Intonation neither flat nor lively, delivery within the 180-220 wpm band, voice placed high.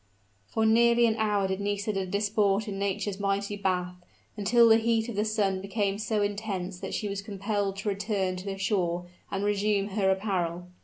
No: narrow, 1.6 semitones; average, 185 wpm; high, 200 Hz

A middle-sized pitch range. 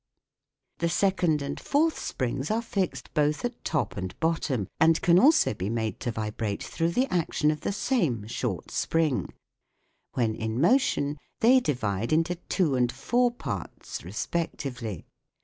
No: wide, 7.5 semitones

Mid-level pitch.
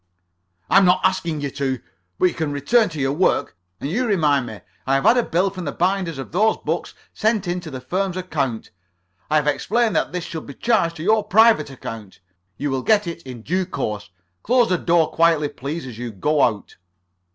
Yes: medium, 165 Hz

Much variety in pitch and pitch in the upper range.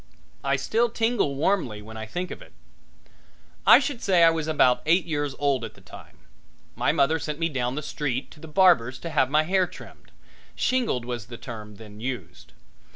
No: wide, 5.7 semitones; medium, 145 Hz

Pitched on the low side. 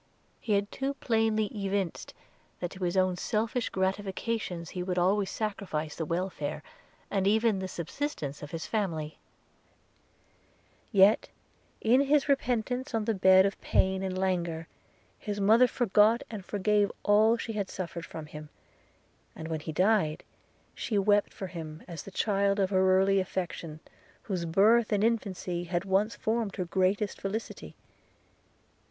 No: high, 195 Hz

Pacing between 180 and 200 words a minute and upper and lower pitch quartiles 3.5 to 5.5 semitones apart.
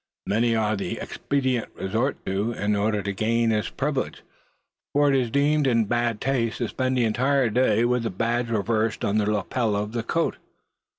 No: average, 185 wpm; average, 3.0 semitones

